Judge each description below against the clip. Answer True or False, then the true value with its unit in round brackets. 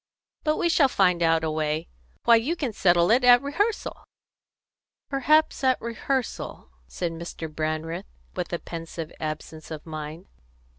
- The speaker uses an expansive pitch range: True (8.5 semitones)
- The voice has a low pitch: False (175 Hz)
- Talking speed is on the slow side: False (145 wpm)